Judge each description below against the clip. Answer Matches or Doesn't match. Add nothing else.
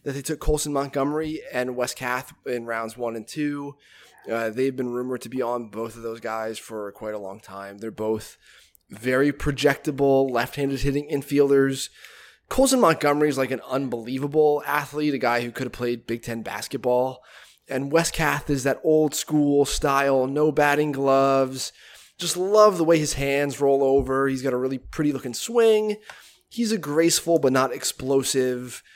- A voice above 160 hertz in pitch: Doesn't match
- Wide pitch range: Doesn't match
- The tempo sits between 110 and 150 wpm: Doesn't match